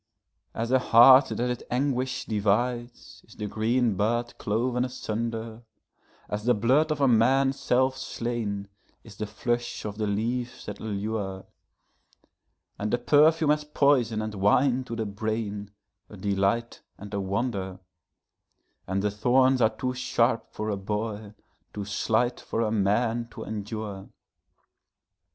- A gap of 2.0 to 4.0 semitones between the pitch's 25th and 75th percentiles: Yes, average, 3.0 semitones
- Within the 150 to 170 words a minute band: No, slow, 135 wpm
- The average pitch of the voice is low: Yes, low, 115 Hz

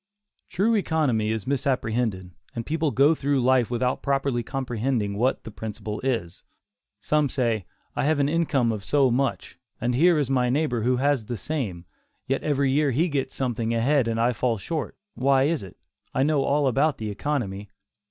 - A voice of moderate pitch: No, low, 130 Hz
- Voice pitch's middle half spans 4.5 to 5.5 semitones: No, average, 3.9 semitones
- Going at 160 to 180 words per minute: Yes, average, 175 wpm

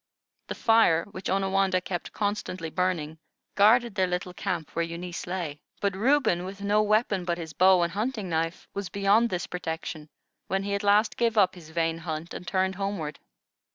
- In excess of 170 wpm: Yes, average, 180 wpm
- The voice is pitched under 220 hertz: Yes, medium, 185 Hz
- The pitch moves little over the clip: No, average, 3.1 semitones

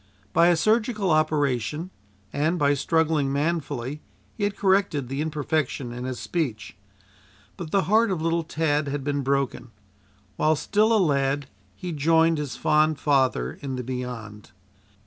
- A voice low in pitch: No, medium, 150 Hz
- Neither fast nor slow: Yes, average, 145 wpm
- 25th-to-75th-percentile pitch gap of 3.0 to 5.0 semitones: Yes, average, 3.5 semitones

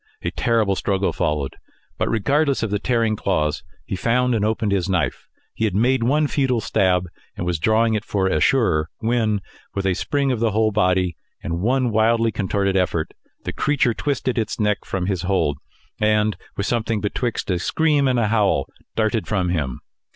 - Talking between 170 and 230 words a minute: Yes, average, 185 wpm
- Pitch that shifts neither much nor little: Yes, average, 3.7 semitones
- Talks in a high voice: No, low, 105 Hz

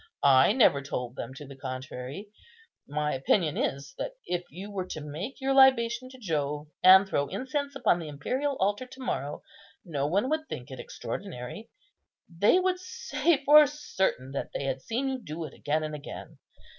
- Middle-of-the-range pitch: Yes, medium, 180 Hz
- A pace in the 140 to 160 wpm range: No, average, 180 wpm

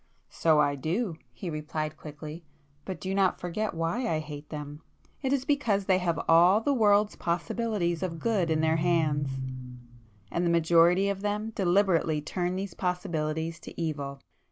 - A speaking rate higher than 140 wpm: Yes, average, 155 wpm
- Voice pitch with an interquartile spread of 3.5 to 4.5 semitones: Yes, average, 4.0 semitones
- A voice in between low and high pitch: Yes, medium, 170 Hz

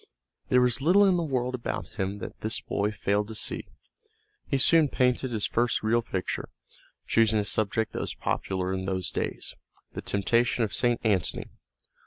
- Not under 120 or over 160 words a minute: No, average, 175 wpm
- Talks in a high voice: No, low, 115 Hz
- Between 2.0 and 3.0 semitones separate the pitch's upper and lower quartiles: No, average, 3.7 semitones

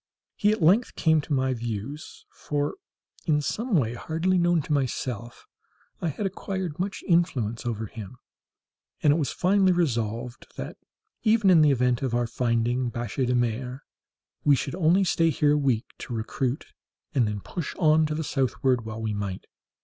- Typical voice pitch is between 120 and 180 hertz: Yes, low, 135 Hz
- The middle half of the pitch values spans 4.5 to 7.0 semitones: Yes, wide, 5.6 semitones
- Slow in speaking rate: No, average, 170 wpm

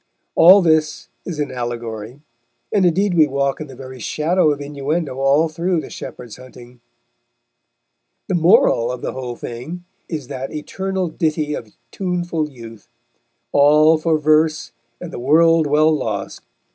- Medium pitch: Yes, medium, 150 Hz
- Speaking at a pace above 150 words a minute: No, average, 145 wpm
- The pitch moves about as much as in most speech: Yes, average, 4.3 semitones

